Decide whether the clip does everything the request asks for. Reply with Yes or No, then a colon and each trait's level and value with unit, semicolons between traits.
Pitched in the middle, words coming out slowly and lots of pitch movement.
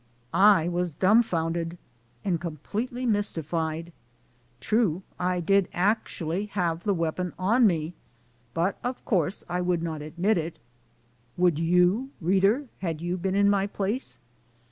No: medium, 180 Hz; slow, 130 wpm; average, 3.3 semitones